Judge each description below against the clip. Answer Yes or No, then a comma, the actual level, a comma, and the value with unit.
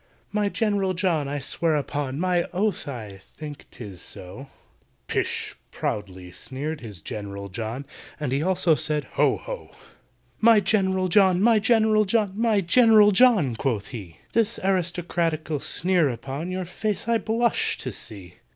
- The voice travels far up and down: Yes, wide, 7.7 semitones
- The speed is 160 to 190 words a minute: No, average, 145 wpm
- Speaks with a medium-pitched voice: Yes, medium, 170 Hz